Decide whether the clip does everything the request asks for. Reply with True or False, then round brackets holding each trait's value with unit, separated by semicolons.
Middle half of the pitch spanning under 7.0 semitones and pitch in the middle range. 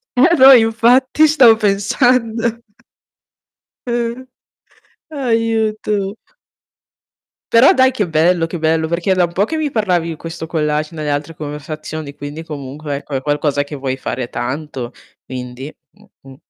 False (7.5 semitones; 170 Hz)